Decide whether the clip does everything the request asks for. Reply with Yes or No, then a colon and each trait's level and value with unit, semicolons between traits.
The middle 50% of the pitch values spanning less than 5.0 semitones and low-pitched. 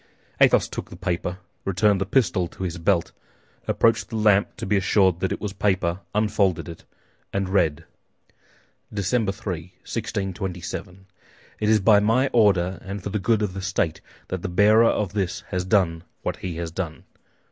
Yes: average, 2.8 semitones; very low, 95 Hz